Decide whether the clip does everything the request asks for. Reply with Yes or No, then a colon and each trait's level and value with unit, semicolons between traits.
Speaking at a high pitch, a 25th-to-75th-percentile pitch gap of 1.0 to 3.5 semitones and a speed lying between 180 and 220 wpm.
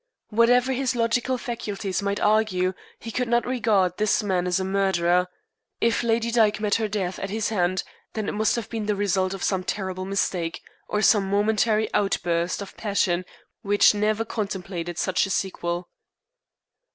No: high, 205 Hz; average, 2.9 semitones; average, 165 wpm